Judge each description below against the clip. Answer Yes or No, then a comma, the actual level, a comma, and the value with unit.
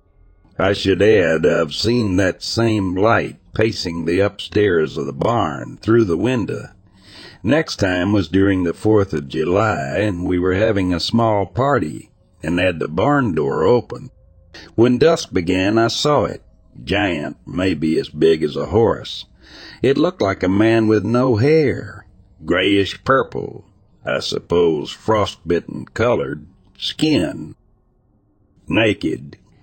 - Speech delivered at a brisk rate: No, slow, 135 wpm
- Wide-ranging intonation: No, average, 3.8 semitones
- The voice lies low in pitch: Yes, low, 100 Hz